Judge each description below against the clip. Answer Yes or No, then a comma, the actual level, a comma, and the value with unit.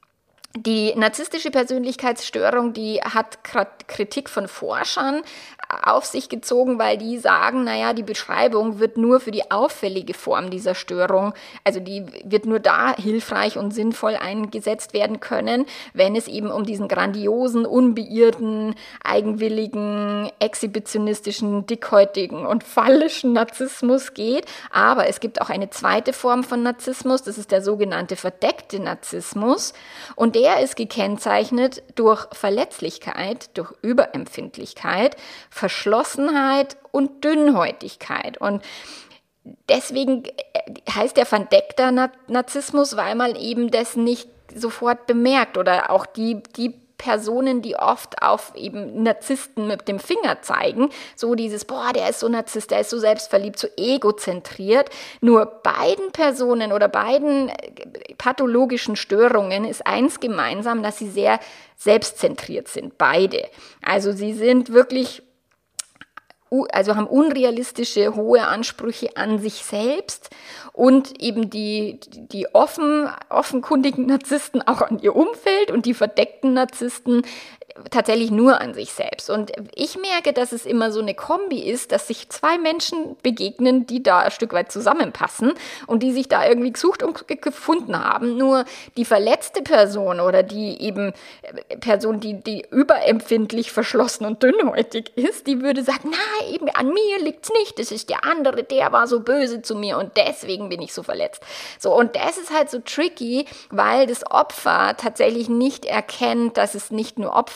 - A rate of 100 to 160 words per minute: Yes, average, 140 wpm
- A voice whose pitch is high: Yes, high, 240 Hz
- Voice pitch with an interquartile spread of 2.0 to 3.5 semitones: No, average, 4.3 semitones